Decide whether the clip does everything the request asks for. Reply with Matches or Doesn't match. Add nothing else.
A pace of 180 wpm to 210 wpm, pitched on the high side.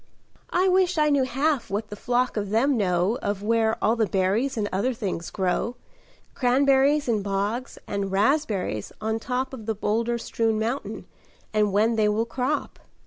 Doesn't match